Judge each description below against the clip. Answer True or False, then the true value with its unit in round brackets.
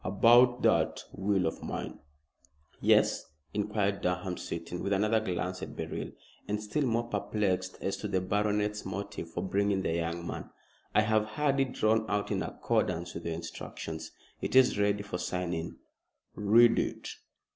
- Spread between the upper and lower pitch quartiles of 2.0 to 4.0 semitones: True (3.0 semitones)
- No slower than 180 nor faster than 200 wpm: False (160 wpm)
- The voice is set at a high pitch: False (100 Hz)